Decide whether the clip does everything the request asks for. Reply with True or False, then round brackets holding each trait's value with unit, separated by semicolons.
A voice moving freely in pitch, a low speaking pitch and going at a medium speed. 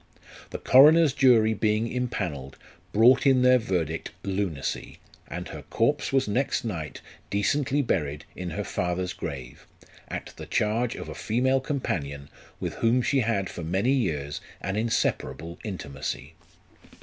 True (6.9 semitones; 105 Hz; 145 wpm)